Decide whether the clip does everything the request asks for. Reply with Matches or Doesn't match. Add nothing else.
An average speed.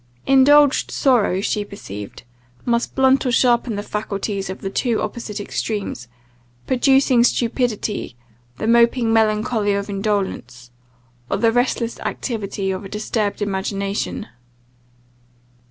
Doesn't match